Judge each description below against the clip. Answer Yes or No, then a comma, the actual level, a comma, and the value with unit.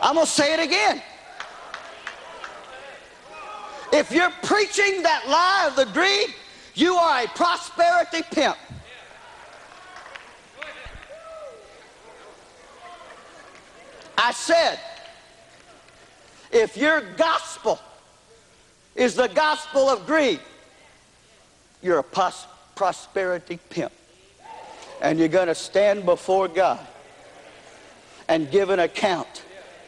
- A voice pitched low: No, very high, 320 Hz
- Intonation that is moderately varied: No, wide, 5.9 semitones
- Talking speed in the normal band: No, slow, 90 wpm